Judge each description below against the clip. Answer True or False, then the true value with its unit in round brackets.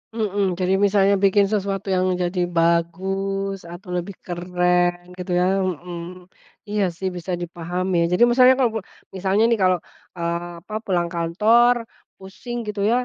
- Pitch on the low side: False (190 Hz)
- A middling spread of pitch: False (2.3 semitones)